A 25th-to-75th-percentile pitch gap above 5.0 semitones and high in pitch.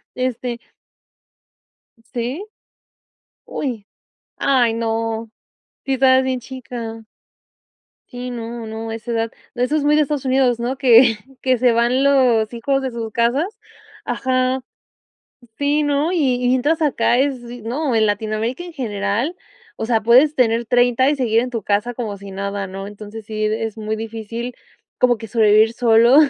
No: average, 2.7 semitones; high, 240 Hz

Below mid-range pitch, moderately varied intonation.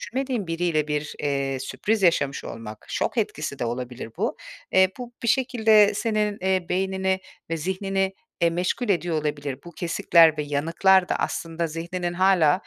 No: medium, 175 Hz; average, 4.2 semitones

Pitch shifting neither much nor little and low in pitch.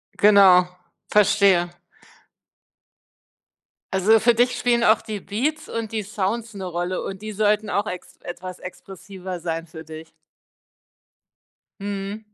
No: average, 3.0 semitones; high, 200 Hz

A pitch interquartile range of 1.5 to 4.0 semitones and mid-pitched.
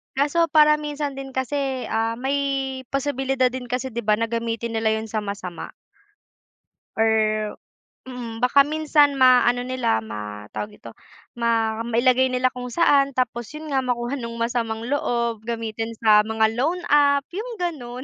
No: average, 3.4 semitones; very high, 250 Hz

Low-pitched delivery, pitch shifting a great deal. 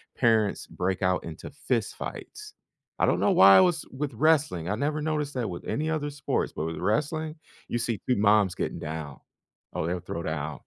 Yes: low, 110 Hz; wide, 8.5 semitones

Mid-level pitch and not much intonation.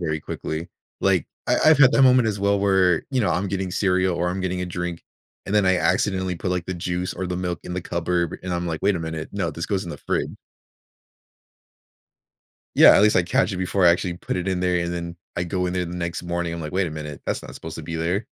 No: very low, 90 Hz; narrow, 1.9 semitones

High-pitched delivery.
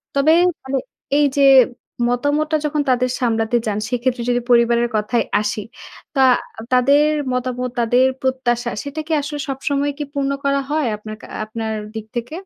Yes: very high, 250 Hz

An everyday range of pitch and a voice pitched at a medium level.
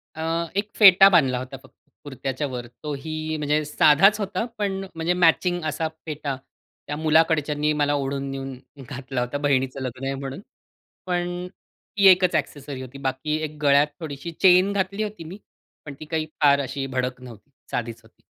Yes: average, 4.3 semitones; medium, 150 Hz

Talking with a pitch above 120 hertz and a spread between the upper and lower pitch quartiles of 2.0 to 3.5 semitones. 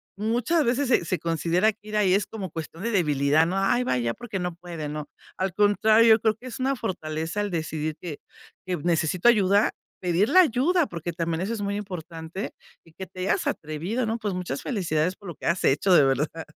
No: medium, 185 Hz; average, 5.0 semitones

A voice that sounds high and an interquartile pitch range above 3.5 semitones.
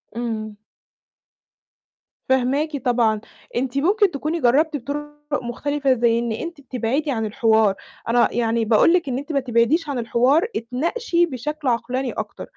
Yes: very high, 260 Hz; average, 4.1 semitones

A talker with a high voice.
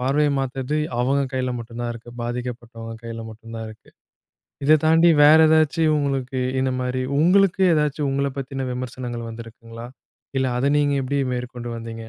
No: low, 130 Hz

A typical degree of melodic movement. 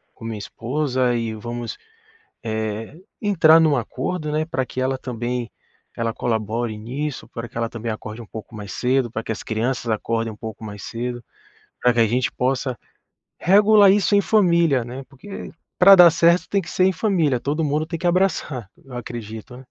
No: wide, 5.7 semitones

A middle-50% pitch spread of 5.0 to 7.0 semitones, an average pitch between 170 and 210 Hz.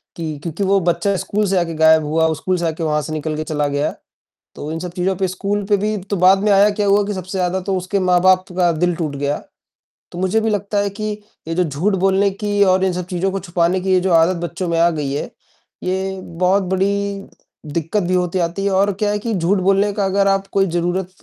No: average, 2.7 semitones; medium, 185 Hz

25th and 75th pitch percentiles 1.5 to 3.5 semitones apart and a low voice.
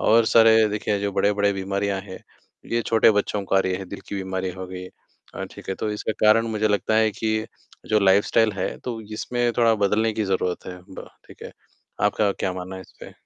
Yes: narrow, 2.4 semitones; low, 105 Hz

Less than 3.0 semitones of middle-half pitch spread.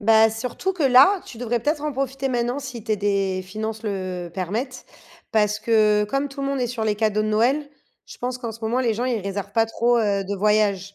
No: average, 3.3 semitones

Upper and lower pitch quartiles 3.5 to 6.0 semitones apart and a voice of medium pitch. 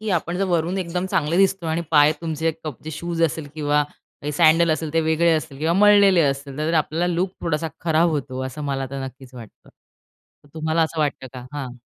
No: average, 2.7 semitones; medium, 160 Hz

